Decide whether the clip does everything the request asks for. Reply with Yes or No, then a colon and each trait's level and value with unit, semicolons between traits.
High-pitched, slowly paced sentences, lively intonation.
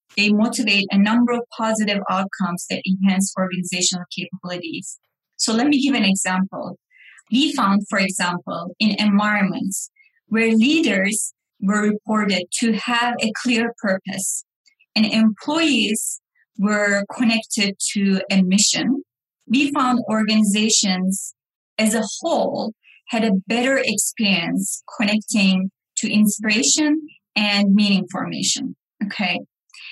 No: high, 215 Hz; slow, 110 wpm; average, 3.3 semitones